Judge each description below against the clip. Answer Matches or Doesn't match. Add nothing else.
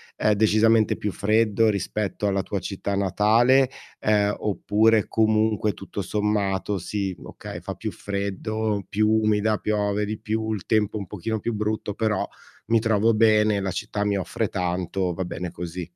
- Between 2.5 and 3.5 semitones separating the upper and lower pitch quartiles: Doesn't match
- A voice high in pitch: Doesn't match